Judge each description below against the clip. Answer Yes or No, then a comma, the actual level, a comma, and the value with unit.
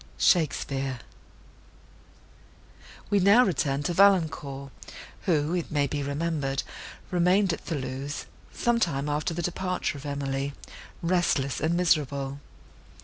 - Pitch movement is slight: No, average, 4.2 semitones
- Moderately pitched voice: Yes, medium, 150 Hz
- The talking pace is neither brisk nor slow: No, slow, 110 wpm